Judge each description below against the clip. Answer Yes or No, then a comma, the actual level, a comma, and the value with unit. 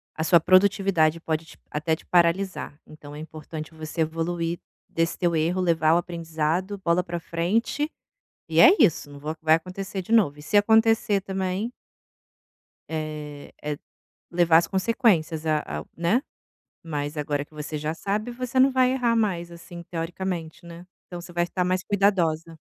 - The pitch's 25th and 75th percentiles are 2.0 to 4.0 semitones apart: Yes, average, 3.4 semitones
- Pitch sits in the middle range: Yes, medium, 170 Hz